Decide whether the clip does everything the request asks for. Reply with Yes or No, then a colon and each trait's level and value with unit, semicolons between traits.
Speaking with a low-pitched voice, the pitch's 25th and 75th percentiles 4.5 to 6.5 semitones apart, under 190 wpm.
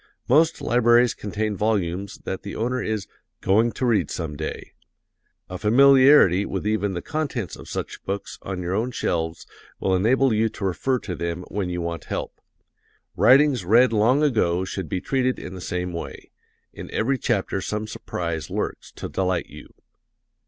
Yes: low, 105 Hz; average, 5.2 semitones; average, 165 wpm